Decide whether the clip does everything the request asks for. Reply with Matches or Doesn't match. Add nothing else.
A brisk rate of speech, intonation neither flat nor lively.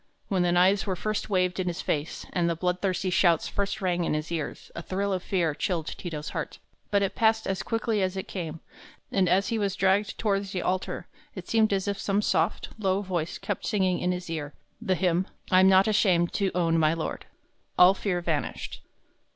Doesn't match